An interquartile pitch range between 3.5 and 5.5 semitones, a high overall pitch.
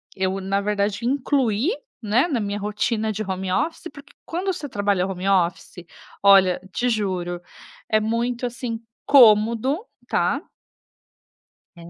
Yes: average, 4.0 semitones; high, 215 Hz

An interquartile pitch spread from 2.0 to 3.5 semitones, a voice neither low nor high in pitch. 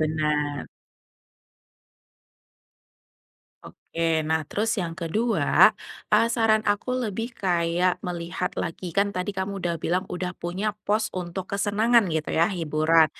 No: average, 3.9 semitones; medium, 180 Hz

